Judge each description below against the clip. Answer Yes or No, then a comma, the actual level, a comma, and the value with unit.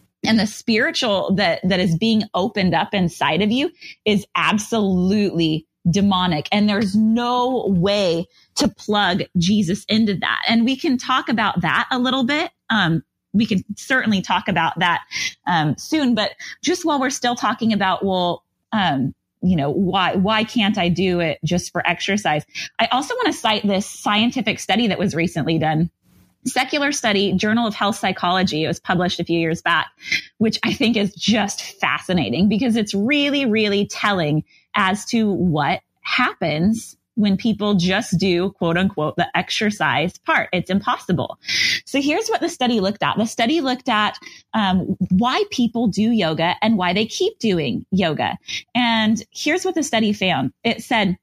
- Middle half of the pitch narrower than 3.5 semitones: No, average, 4.0 semitones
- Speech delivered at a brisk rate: No, average, 165 wpm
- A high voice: Yes, high, 210 Hz